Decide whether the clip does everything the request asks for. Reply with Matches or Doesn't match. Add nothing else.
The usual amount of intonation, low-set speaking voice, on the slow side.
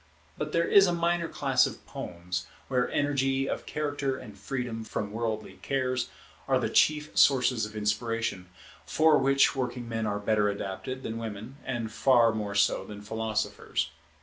Doesn't match